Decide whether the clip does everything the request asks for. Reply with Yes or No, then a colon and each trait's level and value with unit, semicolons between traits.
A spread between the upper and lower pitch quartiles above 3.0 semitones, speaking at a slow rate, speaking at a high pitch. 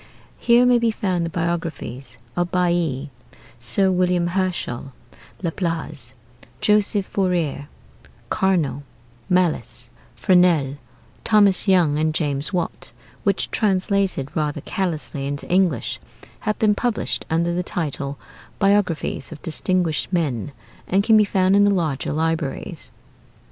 No: average, 4.2 semitones; slow, 115 wpm; medium, 175 Hz